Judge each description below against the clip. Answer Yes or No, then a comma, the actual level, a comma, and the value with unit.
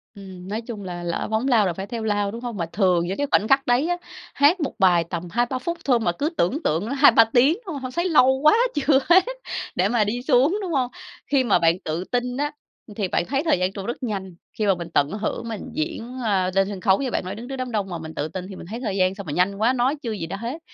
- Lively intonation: Yes, wide, 5.7 semitones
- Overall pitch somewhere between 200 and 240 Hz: Yes, high, 220 Hz